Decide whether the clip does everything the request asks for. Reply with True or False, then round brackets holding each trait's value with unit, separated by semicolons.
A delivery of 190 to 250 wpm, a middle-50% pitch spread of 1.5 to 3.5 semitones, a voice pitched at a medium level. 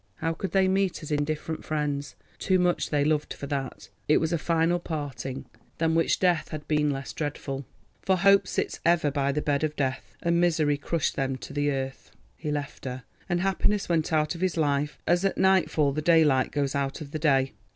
True (200 wpm; 3.1 semitones; 150 Hz)